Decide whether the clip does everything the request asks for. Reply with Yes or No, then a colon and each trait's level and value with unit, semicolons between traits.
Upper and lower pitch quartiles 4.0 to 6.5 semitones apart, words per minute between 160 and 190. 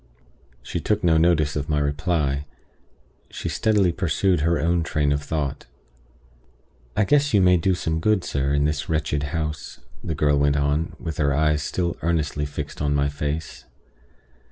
No: average, 3.0 semitones; average, 165 wpm